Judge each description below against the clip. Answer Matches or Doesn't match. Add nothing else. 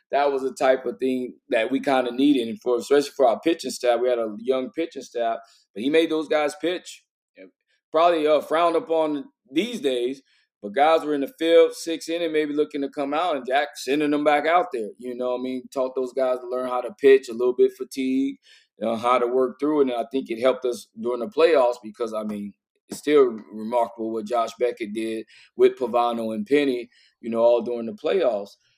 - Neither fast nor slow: Doesn't match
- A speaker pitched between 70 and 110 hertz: Doesn't match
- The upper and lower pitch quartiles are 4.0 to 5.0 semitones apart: Matches